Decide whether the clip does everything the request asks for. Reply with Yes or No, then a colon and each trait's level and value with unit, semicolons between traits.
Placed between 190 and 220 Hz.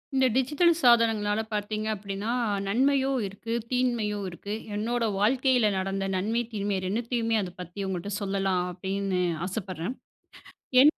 Yes: high, 210 Hz